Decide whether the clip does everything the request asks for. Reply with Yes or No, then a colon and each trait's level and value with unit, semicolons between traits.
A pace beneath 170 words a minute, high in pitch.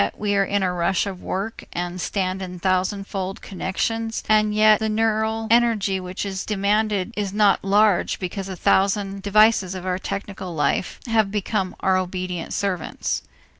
Yes: average, 160 wpm; high, 195 Hz